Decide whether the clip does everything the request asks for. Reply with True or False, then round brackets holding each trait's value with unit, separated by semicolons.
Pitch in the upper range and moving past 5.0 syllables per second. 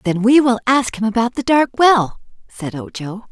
False (230 Hz; 4.9 syllables/s)